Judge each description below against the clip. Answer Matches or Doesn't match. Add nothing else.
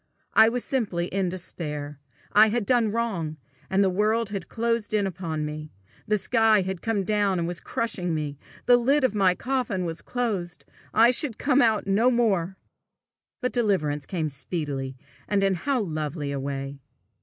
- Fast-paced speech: Doesn't match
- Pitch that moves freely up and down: Matches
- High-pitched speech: Matches